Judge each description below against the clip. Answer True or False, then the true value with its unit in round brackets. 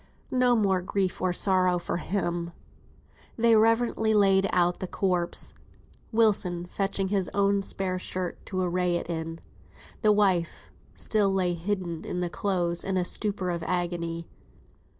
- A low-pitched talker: False (185 Hz)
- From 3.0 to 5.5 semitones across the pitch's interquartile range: False (2.4 semitones)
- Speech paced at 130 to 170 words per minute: True (145 wpm)